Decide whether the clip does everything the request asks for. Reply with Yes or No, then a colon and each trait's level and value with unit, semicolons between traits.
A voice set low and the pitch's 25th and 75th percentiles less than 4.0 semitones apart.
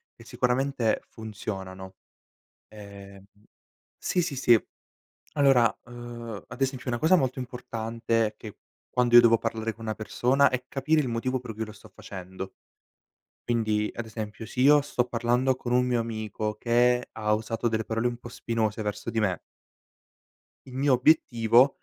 Yes: low, 115 Hz; narrow, 2.5 semitones